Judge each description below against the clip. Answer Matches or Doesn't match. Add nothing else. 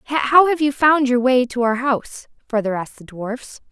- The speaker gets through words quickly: Matches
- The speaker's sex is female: Matches